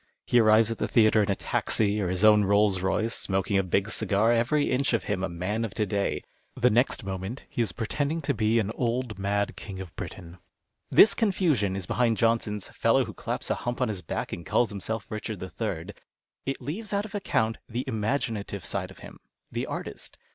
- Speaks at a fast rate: Yes, fast, 210 wpm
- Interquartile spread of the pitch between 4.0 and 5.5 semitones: No, average, 3.5 semitones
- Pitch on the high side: No, low, 110 Hz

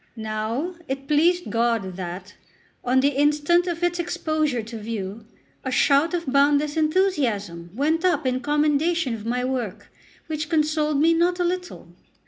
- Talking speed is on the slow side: No, average, 150 wpm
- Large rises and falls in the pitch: Yes, wide, 5.9 semitones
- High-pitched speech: Yes, very high, 290 Hz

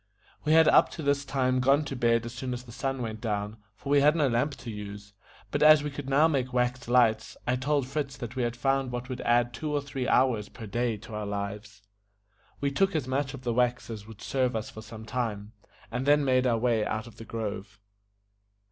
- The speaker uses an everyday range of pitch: Yes, average, 3.5 semitones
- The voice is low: Yes, low, 125 Hz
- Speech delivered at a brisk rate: Yes, fast, 235 wpm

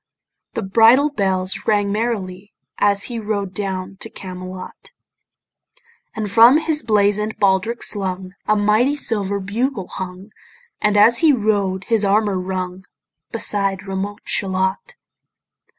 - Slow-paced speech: Yes, slow, 120 wpm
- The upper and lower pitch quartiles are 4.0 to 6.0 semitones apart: No, narrow, 2.6 semitones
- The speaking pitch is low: No, high, 205 Hz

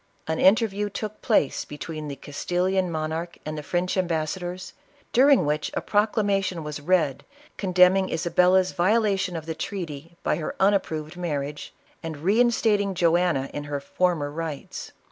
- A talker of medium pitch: Yes, medium, 175 Hz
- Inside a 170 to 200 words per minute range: No, average, 145 wpm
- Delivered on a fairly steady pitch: No, average, 3.8 semitones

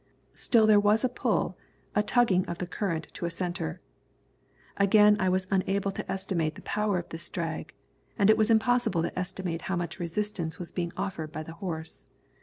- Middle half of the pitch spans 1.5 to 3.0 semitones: No, average, 3.6 semitones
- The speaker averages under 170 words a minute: No, average, 190 wpm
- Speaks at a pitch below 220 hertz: Yes, medium, 185 Hz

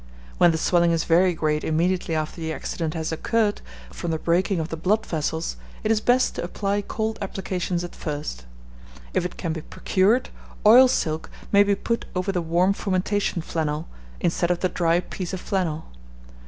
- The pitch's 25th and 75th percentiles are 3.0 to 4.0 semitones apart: Yes, average, 3.4 semitones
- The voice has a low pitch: No, medium, 175 Hz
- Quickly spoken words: No, average, 180 wpm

